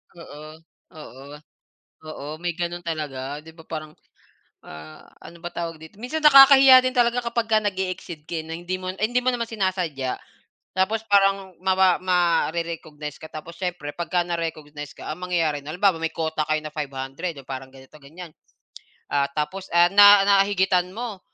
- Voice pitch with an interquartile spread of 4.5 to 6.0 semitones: No, average, 3.9 semitones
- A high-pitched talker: No, medium, 170 Hz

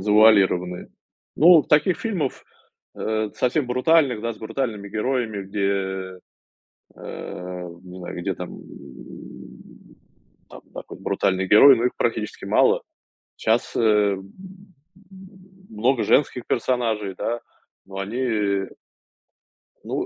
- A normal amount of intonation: Yes, average, 4.3 semitones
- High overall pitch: No, low, 110 Hz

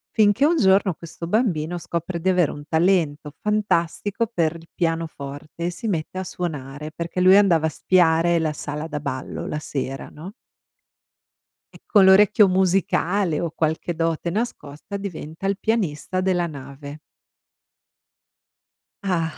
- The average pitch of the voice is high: No, medium, 170 Hz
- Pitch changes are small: No, average, 3.6 semitones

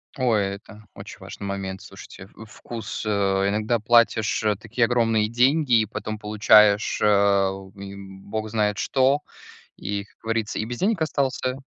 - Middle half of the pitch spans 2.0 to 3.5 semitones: Yes, average, 2.9 semitones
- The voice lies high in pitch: No, low, 110 Hz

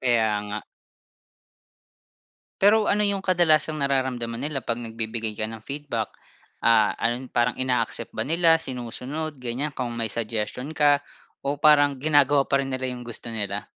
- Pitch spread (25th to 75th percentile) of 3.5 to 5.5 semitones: Yes, average, 4.1 semitones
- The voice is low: Yes, low, 130 Hz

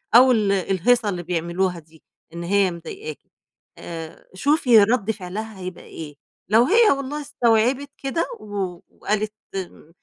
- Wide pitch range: Yes, wide, 5.9 semitones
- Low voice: No, high, 205 Hz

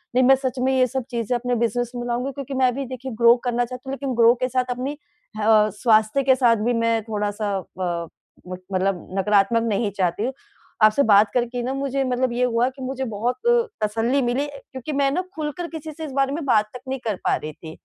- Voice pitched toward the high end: Yes, high, 245 Hz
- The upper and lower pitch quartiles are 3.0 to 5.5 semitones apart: Yes, average, 3.5 semitones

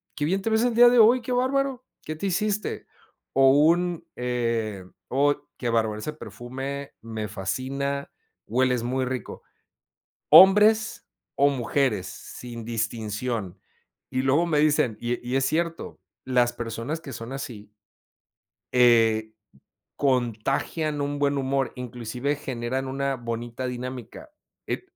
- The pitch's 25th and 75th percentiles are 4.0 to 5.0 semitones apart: Yes, average, 4.3 semitones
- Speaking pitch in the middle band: No, low, 130 Hz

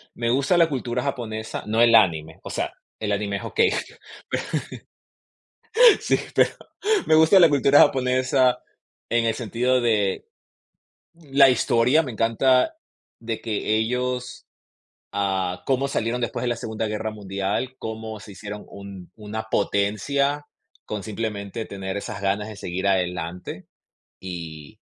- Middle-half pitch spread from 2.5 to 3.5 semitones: No, average, 4.0 semitones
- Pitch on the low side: Yes, low, 110 Hz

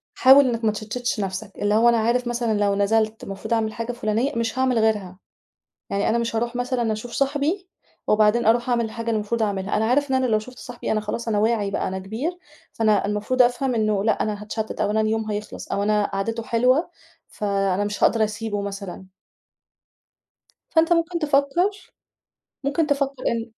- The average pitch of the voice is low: No, high, 225 Hz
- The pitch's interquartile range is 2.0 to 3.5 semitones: Yes, average, 2.9 semitones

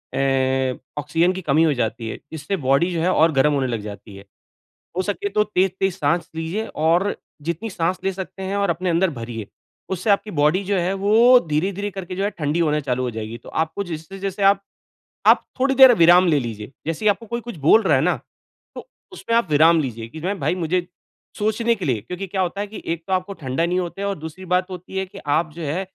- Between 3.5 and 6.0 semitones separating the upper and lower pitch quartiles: Yes, average, 4.7 semitones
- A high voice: No, medium, 175 Hz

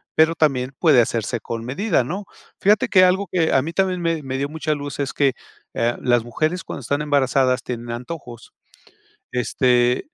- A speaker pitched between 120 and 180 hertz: Yes, medium, 140 Hz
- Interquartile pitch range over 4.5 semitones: Yes, average, 5.0 semitones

